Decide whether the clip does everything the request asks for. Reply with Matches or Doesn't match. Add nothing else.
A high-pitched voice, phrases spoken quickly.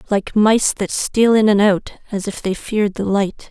Matches